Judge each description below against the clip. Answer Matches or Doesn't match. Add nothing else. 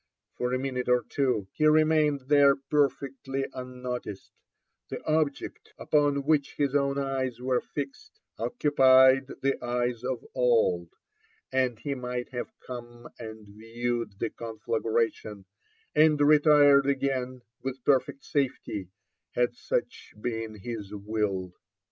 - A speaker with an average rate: Doesn't match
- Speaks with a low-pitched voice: Matches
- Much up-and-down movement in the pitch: Doesn't match